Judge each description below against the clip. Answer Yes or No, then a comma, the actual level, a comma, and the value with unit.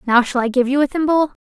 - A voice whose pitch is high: Yes, very high, 265 Hz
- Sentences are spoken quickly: Yes, fast, 290 wpm